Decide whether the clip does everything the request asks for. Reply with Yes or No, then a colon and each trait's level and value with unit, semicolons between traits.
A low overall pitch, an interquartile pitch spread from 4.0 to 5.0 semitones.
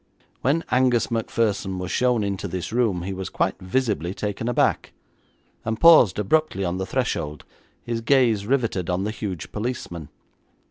Yes: low, 105 Hz; average, 4.7 semitones